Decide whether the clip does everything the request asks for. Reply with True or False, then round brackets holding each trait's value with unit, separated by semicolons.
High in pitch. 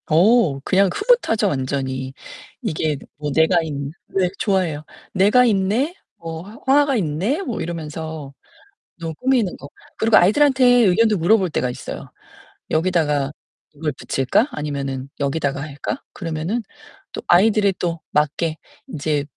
False (165 Hz)